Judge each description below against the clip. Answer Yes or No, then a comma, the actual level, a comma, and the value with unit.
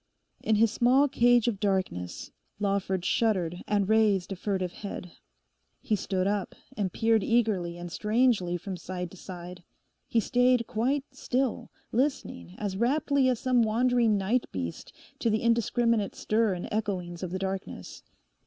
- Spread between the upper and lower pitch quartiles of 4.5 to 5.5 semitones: No, average, 4.1 semitones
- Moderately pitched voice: No, high, 210 Hz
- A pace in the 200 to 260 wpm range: No, average, 150 wpm